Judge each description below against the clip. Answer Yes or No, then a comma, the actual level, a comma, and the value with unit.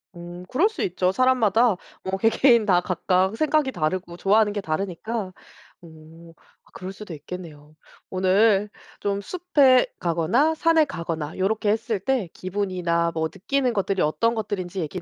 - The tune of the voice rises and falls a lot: No, average, 4.6 semitones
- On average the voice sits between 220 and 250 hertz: No, high, 195 Hz